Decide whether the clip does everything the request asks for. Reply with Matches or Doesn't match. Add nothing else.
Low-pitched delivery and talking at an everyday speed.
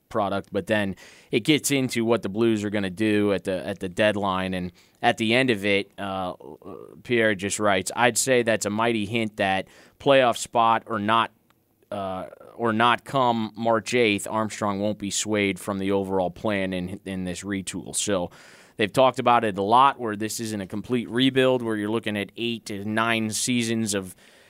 Matches